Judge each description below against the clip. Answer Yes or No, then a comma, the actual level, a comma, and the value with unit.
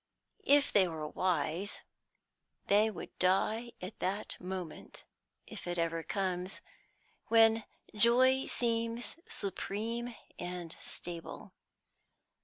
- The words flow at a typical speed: No, slow, 95 wpm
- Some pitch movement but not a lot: Yes, average, 4.3 semitones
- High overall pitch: Yes, high, 200 Hz